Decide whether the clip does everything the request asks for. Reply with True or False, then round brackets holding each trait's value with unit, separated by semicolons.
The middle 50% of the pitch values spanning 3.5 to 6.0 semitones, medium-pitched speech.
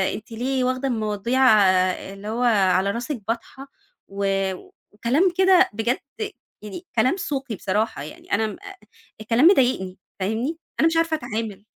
False (4.2 semitones; 230 Hz)